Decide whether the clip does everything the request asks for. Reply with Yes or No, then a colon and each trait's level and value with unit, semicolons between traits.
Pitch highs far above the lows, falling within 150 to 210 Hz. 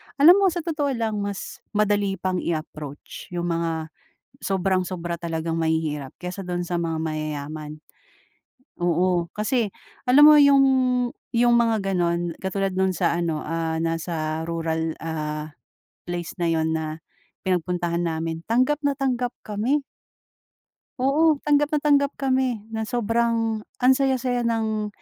Yes: wide, 6.4 semitones; medium, 185 Hz